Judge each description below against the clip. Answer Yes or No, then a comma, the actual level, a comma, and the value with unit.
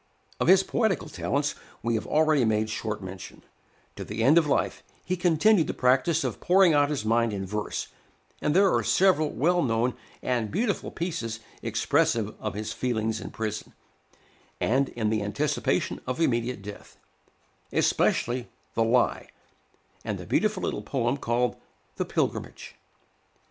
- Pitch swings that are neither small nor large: No, wide, 6.1 semitones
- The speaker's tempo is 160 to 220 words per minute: No, average, 150 wpm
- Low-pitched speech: Yes, low, 125 Hz